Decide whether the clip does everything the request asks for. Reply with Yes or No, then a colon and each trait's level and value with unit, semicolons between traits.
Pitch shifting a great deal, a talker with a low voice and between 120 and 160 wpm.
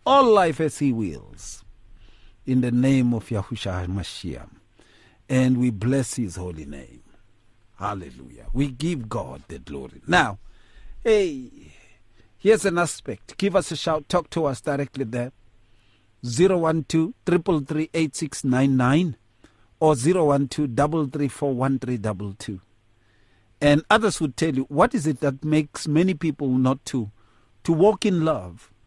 Yes: wide, 6.6 semitones; low, 130 Hz; average, 140 wpm